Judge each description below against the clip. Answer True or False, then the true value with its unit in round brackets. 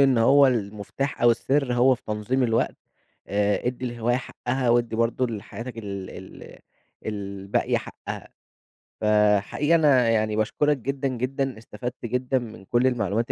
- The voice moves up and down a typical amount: True (3.3 semitones)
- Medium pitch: False (120 Hz)